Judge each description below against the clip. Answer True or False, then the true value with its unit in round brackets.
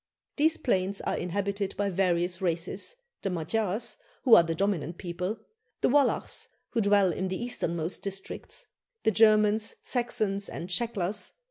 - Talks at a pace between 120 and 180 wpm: True (140 wpm)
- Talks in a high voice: True (195 Hz)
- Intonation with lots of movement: False (3.1 semitones)